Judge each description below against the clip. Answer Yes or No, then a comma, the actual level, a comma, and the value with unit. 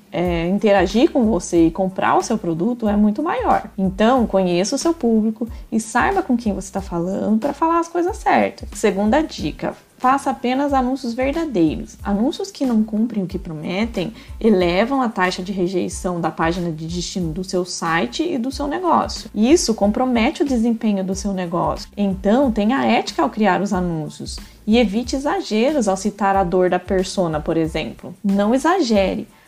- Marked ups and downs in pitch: Yes, wide, 5.7 semitones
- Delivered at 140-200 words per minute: Yes, average, 175 wpm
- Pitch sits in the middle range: No, high, 205 Hz